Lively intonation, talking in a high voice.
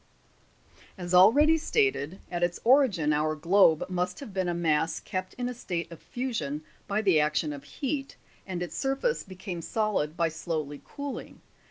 No: wide, 6.4 semitones; medium, 180 Hz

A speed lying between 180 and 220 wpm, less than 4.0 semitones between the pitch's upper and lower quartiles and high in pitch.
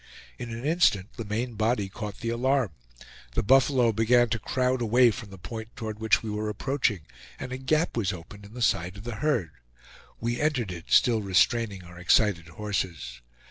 No: average, 185 wpm; average, 3.5 semitones; low, 110 Hz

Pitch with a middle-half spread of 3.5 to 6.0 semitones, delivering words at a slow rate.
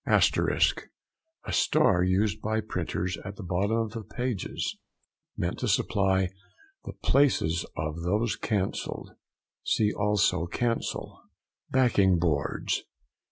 Yes: average, 3.9 semitones; slow, 110 wpm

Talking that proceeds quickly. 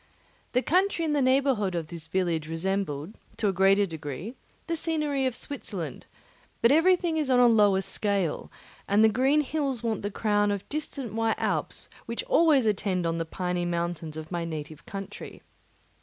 No: average, 170 wpm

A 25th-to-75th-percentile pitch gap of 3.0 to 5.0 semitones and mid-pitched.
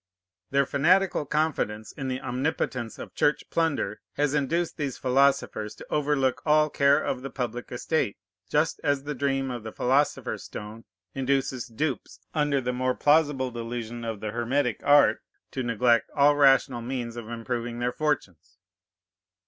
No: average, 3.4 semitones; low, 130 Hz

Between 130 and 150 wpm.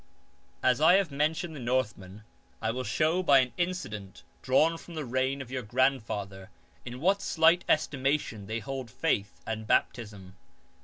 No: average, 160 wpm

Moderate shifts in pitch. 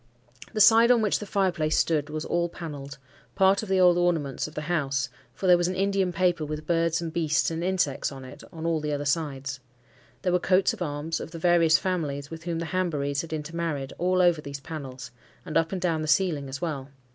Yes: average, 3.5 semitones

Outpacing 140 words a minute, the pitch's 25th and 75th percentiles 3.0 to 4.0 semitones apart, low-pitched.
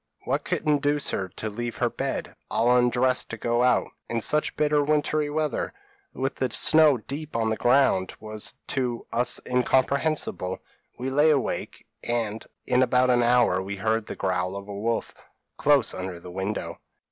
No: average, 175 wpm; average, 4.4 semitones; low, 120 Hz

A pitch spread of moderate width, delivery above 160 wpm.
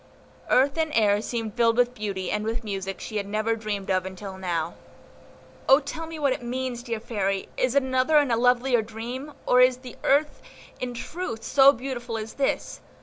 Yes: average, 3.5 semitones; average, 195 wpm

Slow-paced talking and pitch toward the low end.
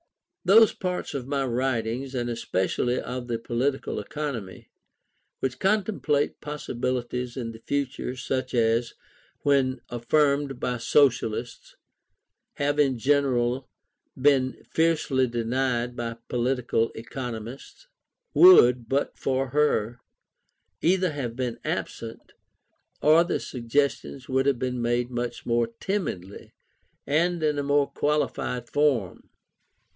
Yes: slow, 110 wpm; low, 130 Hz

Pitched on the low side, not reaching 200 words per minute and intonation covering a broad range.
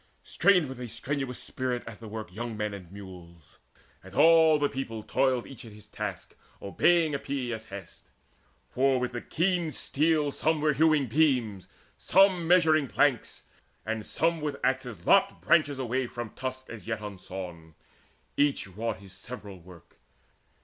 Yes: low, 125 Hz; average, 155 wpm; wide, 6.0 semitones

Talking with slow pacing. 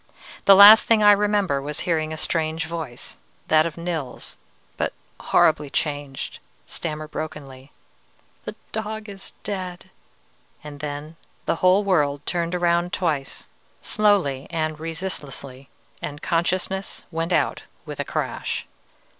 Yes: slow, 125 wpm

